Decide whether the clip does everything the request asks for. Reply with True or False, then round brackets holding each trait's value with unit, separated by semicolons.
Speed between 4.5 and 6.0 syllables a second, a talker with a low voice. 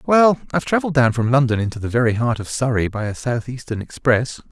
False (6.2 syllables/s; 125 Hz)